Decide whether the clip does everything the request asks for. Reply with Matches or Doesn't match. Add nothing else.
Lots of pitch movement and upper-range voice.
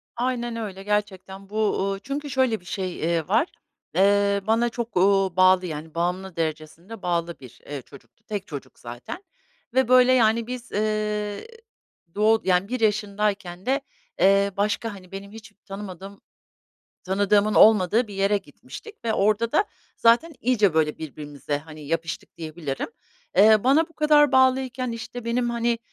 Doesn't match